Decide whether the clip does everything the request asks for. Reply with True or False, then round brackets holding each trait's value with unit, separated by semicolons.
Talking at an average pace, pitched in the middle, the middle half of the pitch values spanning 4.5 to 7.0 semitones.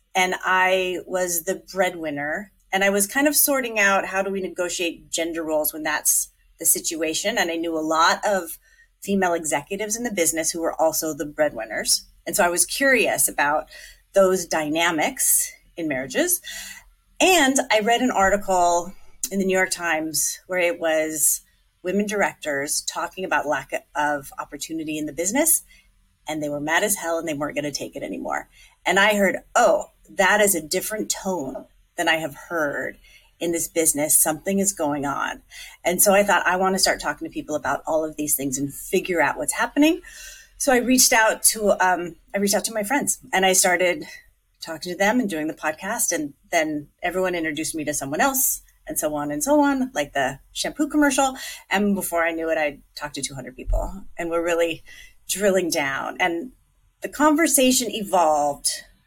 True (190 wpm; 180 Hz; 5.3 semitones)